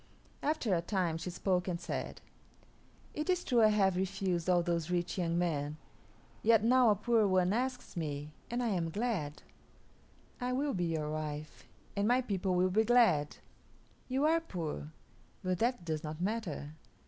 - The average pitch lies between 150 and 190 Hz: Yes, medium, 185 Hz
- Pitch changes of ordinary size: No, wide, 5.7 semitones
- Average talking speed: Yes, average, 170 wpm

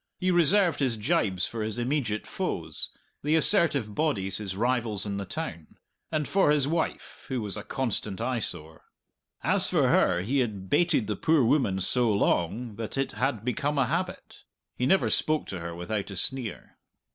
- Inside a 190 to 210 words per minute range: No, average, 175 wpm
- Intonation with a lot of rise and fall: Yes, wide, 6.6 semitones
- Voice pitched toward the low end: Yes, low, 120 Hz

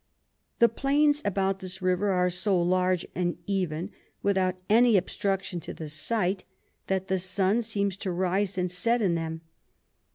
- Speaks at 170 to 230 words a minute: No, average, 155 wpm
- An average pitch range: No, narrow, 2.1 semitones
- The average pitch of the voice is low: No, high, 190 Hz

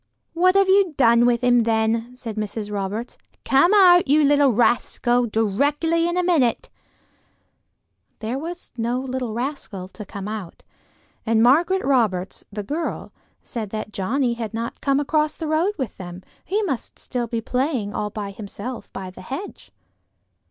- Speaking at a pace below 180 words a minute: Yes, average, 160 wpm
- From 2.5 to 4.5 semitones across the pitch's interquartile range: No, wide, 5.5 semitones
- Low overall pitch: No, high, 245 Hz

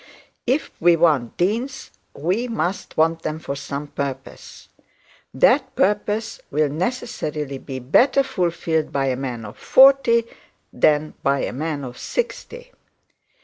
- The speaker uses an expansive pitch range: Yes, wide, 8.6 semitones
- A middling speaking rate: No, slow, 130 wpm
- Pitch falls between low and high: Yes, medium, 160 Hz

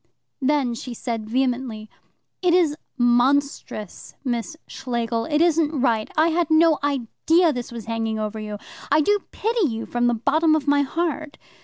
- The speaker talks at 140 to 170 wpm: Yes, average, 165 wpm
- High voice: Yes, very high, 270 Hz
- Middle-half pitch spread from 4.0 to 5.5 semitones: Yes, average, 5.2 semitones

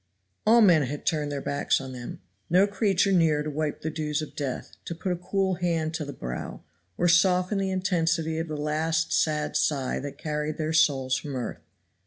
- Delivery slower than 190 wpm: No, average, 200 wpm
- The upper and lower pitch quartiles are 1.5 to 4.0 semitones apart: Yes, average, 3.2 semitones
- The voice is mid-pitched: Yes, medium, 155 Hz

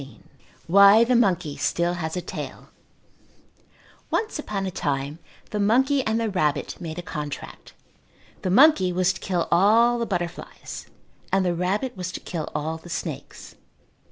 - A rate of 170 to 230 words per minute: No, average, 155 wpm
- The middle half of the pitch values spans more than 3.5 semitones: Yes, average, 4.5 semitones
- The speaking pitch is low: No, medium, 185 Hz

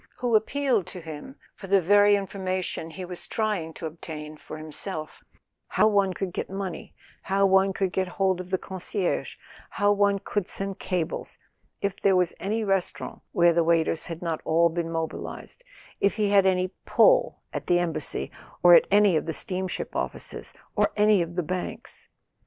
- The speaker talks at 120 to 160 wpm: No, average, 175 wpm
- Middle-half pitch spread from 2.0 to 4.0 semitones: Yes, average, 2.8 semitones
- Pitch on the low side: No, medium, 185 Hz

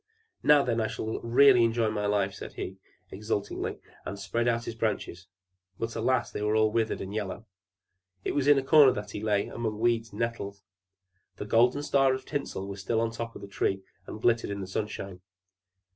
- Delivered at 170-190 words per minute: No, average, 200 wpm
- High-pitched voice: No, low, 110 Hz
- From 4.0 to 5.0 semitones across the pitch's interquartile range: No, narrow, 2.6 semitones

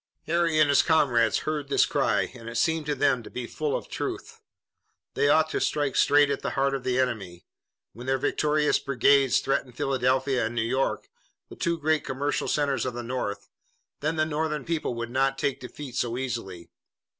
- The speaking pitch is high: No, low, 135 Hz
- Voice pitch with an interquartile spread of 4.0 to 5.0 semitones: No, average, 3.2 semitones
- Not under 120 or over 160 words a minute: No, average, 190 wpm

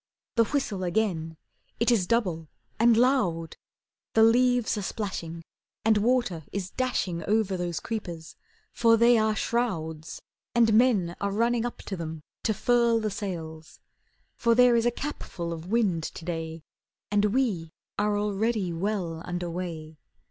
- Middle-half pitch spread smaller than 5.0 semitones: No, wide, 5.5 semitones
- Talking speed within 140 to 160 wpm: Yes, average, 145 wpm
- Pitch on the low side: No, high, 205 Hz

